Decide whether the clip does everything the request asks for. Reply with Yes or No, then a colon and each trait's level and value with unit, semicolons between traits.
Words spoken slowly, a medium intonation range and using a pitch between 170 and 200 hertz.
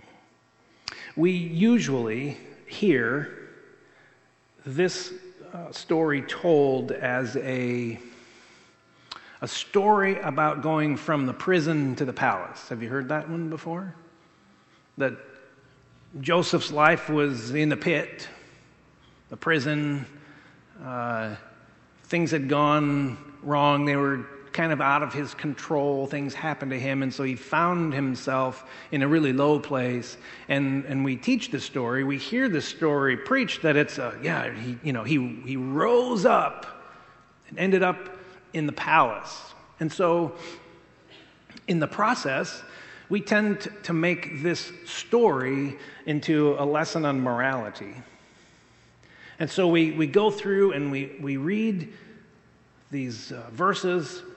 No: slow, 130 wpm; average, 4.1 semitones; medium, 150 Hz